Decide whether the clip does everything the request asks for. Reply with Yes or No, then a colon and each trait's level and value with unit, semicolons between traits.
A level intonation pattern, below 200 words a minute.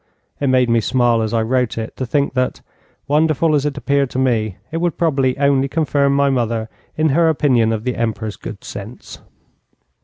No: average, 3.6 semitones; average, 190 wpm